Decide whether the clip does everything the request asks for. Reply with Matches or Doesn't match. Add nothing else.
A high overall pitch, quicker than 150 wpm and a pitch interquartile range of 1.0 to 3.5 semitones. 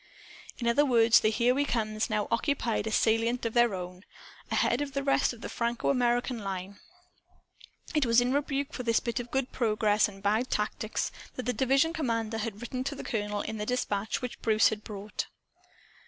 Matches